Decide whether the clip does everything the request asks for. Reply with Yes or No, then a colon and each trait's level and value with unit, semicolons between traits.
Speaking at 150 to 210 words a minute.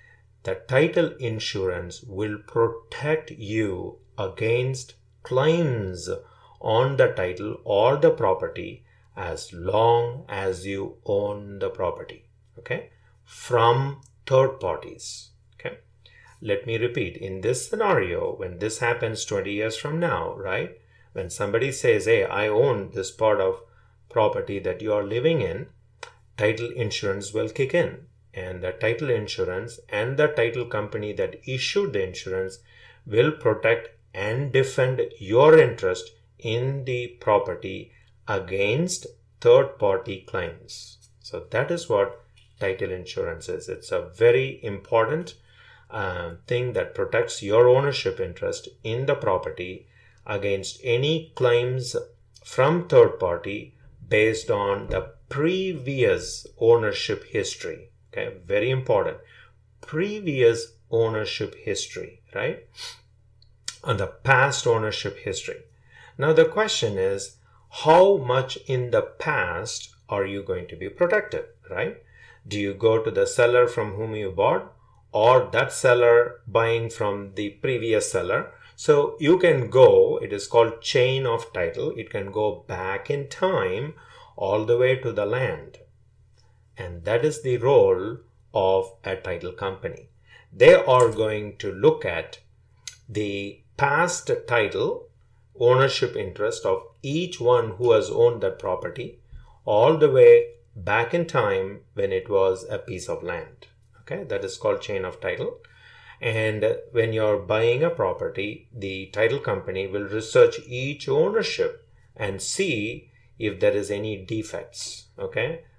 No: slow, 135 wpm